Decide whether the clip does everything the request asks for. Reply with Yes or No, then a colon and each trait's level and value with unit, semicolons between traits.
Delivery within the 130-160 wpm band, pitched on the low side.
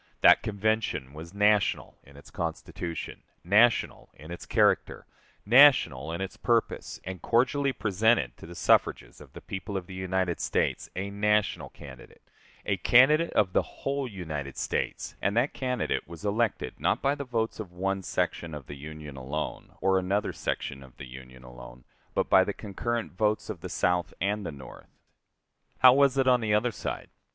No: average, 175 wpm; very low, 95 Hz